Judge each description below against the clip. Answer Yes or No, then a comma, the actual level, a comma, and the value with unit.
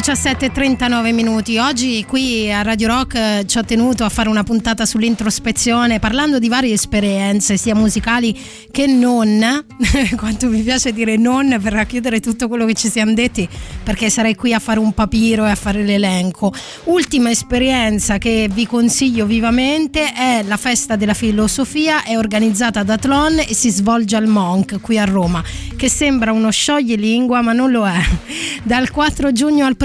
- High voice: Yes, high, 230 Hz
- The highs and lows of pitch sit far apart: No, average, 2.7 semitones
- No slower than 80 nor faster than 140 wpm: No, average, 165 wpm